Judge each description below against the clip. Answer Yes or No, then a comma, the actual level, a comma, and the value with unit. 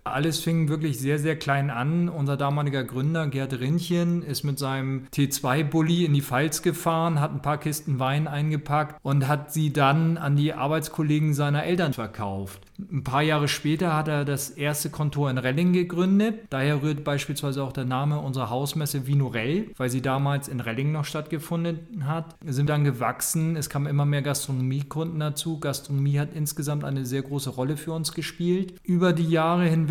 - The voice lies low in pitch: No, medium, 150 Hz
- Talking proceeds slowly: No, average, 185 wpm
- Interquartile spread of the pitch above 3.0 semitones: No, narrow, 2.5 semitones